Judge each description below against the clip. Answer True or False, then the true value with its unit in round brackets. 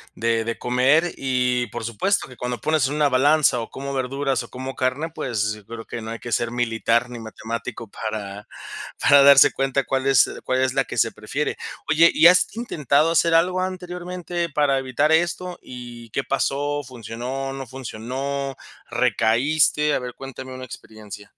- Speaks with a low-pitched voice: True (130 Hz)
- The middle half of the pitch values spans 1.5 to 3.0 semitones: False (3.8 semitones)